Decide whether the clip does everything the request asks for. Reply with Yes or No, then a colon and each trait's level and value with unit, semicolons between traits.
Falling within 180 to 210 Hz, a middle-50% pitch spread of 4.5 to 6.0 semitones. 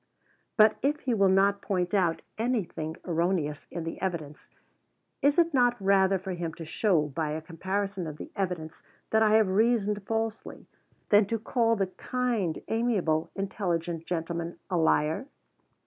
Yes: high, 190 Hz; average, 4.8 semitones